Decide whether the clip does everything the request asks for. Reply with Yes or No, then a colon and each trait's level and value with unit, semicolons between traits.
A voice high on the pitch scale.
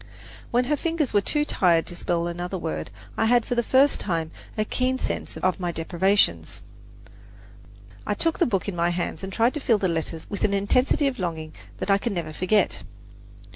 Yes: high, 195 Hz